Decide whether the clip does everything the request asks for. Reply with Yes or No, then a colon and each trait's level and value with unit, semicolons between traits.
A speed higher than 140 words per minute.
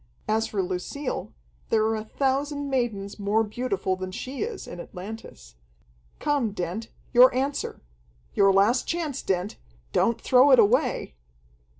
No: slow, 135 wpm